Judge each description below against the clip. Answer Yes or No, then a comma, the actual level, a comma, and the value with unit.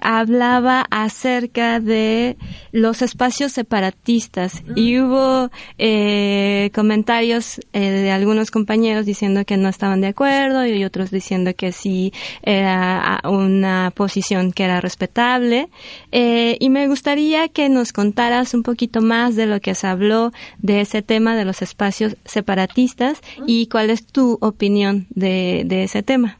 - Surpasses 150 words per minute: No, average, 140 wpm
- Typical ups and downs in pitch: Yes, average, 3.7 semitones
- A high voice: Yes, high, 220 Hz